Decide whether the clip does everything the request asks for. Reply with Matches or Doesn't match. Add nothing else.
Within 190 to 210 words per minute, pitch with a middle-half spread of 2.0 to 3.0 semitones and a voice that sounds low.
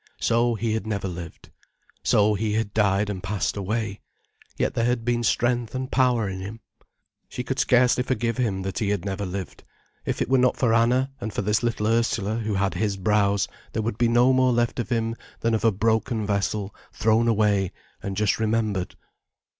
Matches